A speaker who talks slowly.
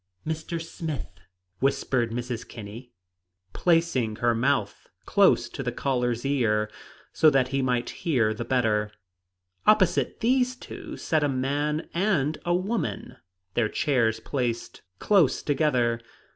Yes: slow, 125 wpm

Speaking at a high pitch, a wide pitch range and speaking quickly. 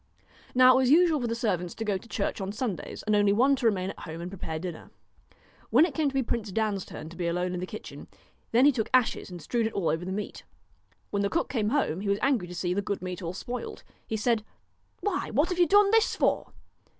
Yes: high, 210 Hz; wide, 5.8 semitones; fast, 255 wpm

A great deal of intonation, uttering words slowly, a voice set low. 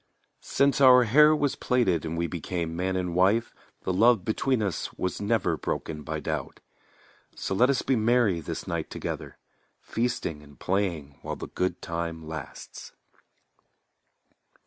No: wide, 6.4 semitones; average, 145 wpm; very low, 95 Hz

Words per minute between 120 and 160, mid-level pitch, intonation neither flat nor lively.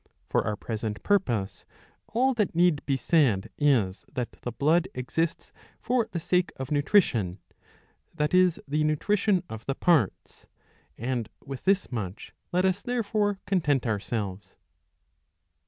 No: average, 140 wpm; medium, 150 Hz; wide, 7.9 semitones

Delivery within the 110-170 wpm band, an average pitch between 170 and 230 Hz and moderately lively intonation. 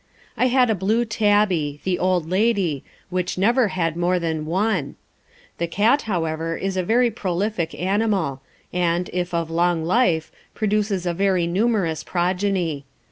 Yes: average, 145 wpm; medium, 185 Hz; average, 3.8 semitones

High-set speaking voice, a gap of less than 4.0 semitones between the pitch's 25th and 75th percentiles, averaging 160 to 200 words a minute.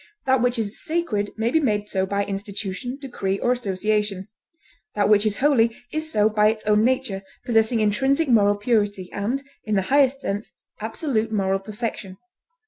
Yes: high, 215 Hz; average, 3.5 semitones; average, 165 wpm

